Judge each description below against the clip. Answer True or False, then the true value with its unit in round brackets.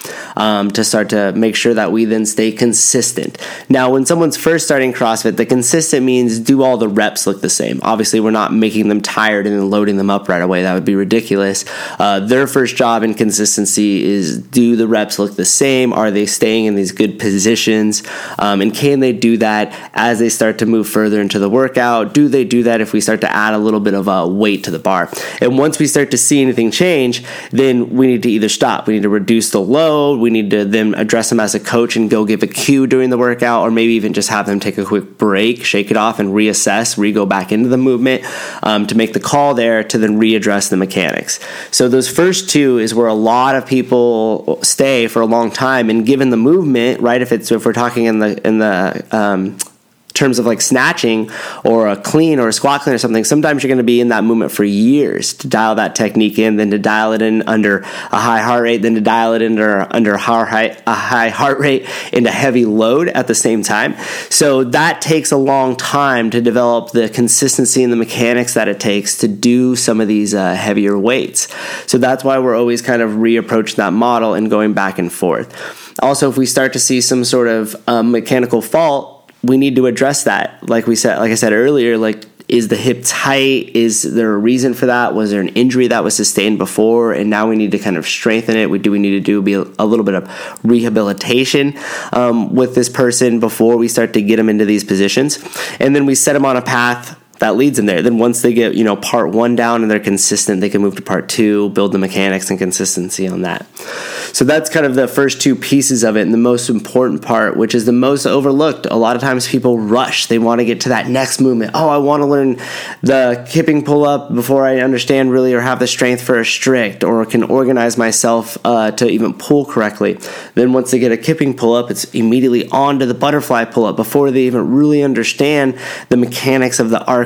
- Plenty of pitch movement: False (3.2 semitones)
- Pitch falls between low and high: False (115 Hz)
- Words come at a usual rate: False (230 wpm)